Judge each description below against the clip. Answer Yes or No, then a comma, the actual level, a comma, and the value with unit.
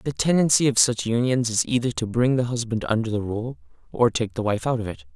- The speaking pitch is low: Yes, low, 120 Hz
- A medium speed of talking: No, fast, 245 wpm